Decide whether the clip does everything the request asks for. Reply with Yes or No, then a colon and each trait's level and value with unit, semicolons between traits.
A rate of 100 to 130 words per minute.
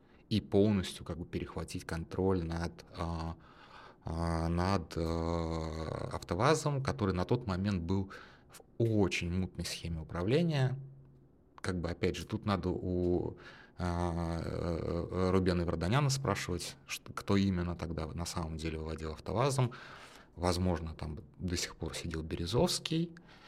Yes: slow, 110 wpm